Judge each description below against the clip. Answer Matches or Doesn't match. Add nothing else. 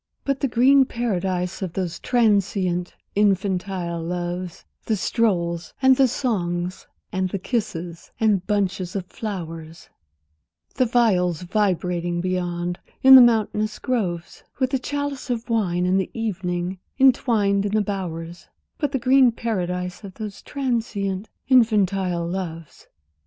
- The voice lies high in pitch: Matches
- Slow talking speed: Matches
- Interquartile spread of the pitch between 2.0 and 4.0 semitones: Doesn't match